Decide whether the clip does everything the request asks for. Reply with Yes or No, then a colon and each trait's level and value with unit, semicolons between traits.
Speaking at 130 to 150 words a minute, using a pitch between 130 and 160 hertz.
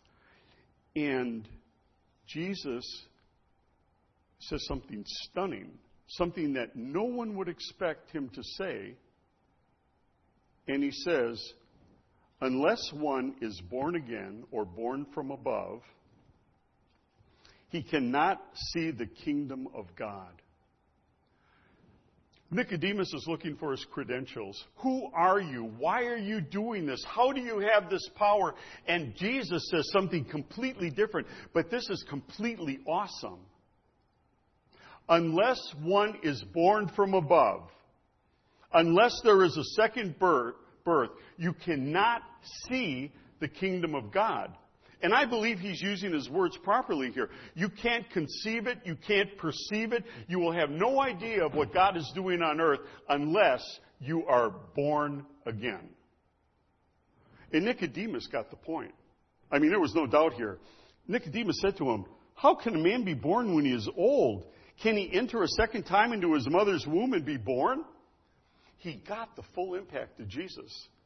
No: average, 140 wpm; medium, 175 Hz